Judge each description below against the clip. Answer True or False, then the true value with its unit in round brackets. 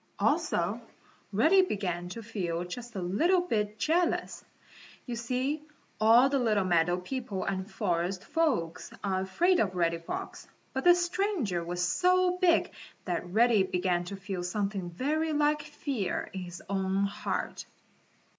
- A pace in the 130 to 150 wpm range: True (145 wpm)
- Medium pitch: False (210 Hz)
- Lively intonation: True (8.5 semitones)